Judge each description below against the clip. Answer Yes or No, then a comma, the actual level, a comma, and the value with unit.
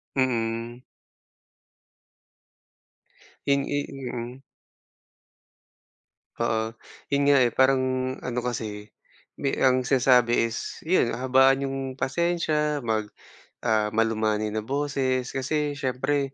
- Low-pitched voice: Yes, low, 130 Hz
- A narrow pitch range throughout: No, average, 3.2 semitones